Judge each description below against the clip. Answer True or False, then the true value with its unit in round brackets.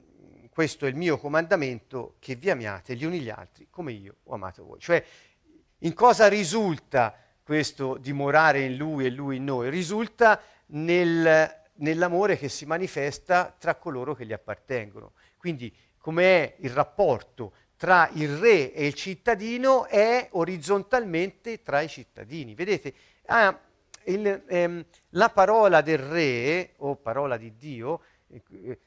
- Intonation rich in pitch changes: True (5.7 semitones)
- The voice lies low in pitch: False (160 Hz)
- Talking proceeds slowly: False (140 wpm)